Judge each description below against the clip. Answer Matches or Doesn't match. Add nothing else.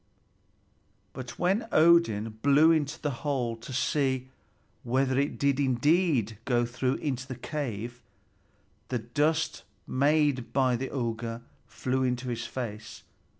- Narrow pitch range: Doesn't match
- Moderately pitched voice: Doesn't match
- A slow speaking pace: Matches